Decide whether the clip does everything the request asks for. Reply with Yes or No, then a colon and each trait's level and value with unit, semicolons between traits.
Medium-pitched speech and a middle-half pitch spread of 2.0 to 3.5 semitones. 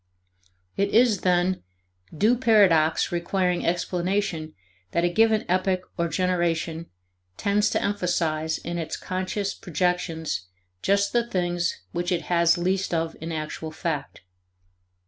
Yes: medium, 175 Hz; average, 2.8 semitones